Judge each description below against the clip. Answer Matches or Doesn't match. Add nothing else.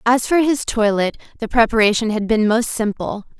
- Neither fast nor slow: Matches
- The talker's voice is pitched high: Matches